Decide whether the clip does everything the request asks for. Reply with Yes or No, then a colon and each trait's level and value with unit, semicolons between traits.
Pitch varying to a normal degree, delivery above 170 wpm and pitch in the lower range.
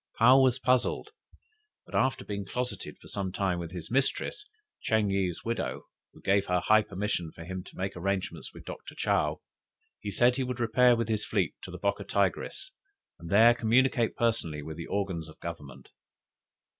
Yes: average, 4.8 semitones; average, 180 wpm; low, 100 Hz